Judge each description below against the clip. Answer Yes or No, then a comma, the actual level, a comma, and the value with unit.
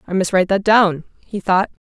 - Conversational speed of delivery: No, fast, 225 wpm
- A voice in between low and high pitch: No, high, 195 Hz